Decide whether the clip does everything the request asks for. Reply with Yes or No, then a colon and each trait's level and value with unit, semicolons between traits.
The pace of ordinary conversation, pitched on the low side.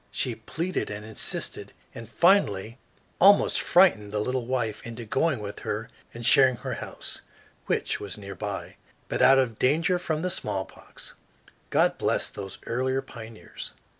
Yes: average, 150 wpm; low, 120 Hz